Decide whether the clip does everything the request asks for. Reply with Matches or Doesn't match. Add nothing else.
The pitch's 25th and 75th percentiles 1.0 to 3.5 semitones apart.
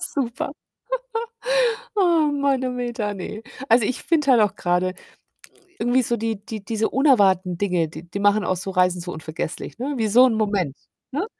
Doesn't match